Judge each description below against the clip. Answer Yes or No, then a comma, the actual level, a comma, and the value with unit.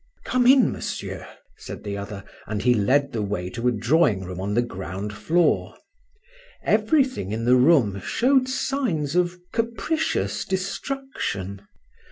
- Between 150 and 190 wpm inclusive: No, average, 140 wpm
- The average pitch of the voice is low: Yes, low, 125 Hz